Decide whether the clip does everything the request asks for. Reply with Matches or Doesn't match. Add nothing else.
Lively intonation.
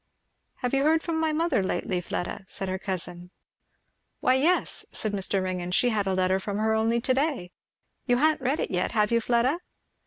Matches